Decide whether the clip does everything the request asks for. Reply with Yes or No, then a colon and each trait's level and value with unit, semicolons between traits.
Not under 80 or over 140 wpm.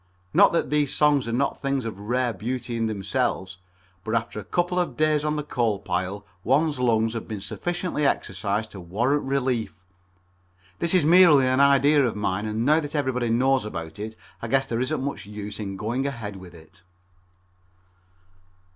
No: average, 175 wpm